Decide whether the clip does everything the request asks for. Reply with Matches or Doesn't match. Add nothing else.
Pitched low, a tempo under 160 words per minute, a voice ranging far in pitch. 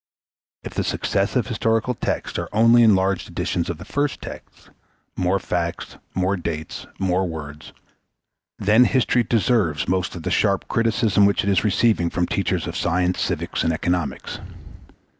Doesn't match